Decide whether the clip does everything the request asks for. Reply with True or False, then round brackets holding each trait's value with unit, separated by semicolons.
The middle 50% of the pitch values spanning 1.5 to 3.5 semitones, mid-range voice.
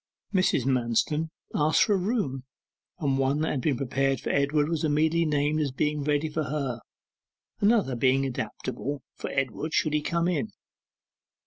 True (2.8 semitones; 145 Hz)